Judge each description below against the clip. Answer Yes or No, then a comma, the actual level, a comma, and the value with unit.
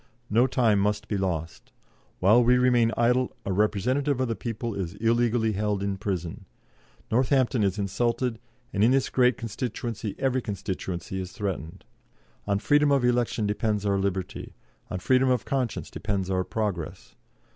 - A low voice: Yes, low, 110 Hz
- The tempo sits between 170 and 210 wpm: No, average, 155 wpm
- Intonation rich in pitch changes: No, average, 3.9 semitones